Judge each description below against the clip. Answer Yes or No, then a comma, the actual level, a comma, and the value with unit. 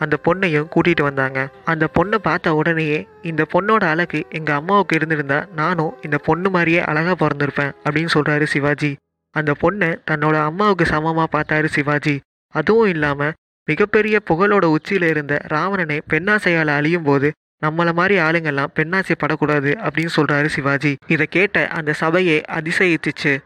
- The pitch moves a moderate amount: No, narrow, 2.3 semitones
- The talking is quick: Yes, fast, 135 wpm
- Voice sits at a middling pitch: Yes, medium, 155 Hz